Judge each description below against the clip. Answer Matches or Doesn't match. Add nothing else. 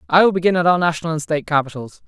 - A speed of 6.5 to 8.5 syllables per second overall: Matches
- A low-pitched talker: Doesn't match